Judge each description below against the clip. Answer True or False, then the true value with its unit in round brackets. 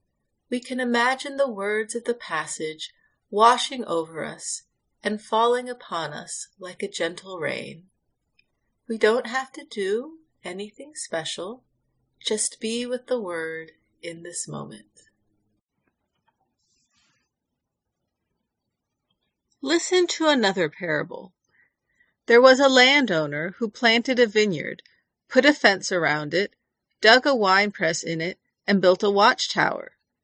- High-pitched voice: True (220 Hz)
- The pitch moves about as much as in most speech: False (5.9 semitones)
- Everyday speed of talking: False (125 wpm)